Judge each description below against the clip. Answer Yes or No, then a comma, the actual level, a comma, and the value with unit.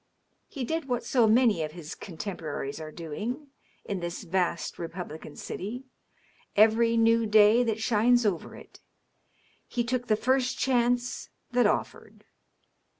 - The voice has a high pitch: Yes, high, 220 Hz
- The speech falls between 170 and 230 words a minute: No, slow, 135 wpm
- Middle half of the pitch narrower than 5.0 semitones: No, wide, 5.6 semitones